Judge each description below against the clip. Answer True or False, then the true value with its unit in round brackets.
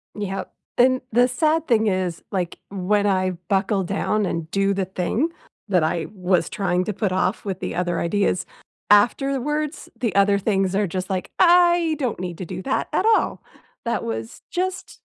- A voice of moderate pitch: False (200 Hz)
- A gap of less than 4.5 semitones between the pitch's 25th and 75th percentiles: False (4.8 semitones)